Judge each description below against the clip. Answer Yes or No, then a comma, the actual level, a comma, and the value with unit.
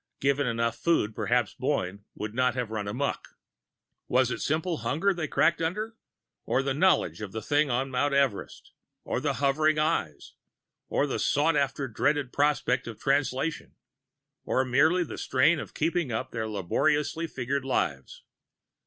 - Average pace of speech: Yes, average, 155 wpm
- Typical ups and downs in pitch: Yes, average, 4.3 semitones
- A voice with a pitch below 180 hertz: Yes, medium, 140 Hz